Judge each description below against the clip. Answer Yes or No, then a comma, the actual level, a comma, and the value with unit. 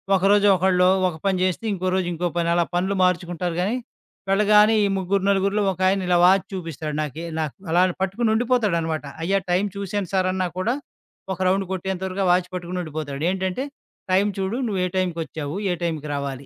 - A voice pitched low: No, medium, 185 Hz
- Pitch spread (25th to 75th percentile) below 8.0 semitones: Yes, narrow, 2.4 semitones